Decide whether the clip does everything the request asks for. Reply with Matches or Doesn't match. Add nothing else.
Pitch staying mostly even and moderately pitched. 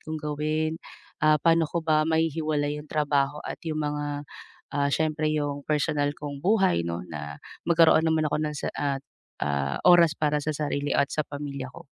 Matches